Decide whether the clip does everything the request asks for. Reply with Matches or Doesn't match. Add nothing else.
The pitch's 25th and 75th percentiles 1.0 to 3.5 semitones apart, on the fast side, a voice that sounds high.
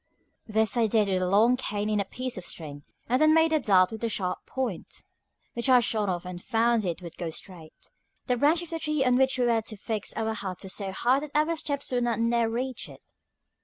Doesn't match